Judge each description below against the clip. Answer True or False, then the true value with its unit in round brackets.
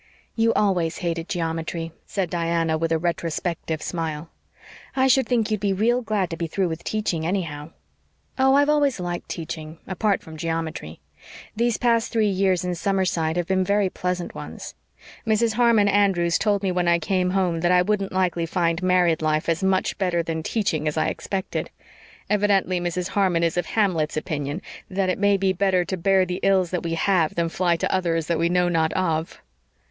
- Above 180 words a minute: True (190 wpm)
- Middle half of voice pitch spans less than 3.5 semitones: True (3.0 semitones)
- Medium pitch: True (180 Hz)